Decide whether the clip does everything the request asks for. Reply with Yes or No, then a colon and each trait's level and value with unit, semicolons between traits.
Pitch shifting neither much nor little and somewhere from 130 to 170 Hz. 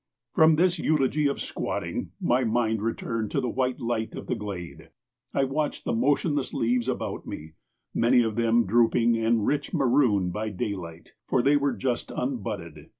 No: average, 3.7 semitones; low, 120 Hz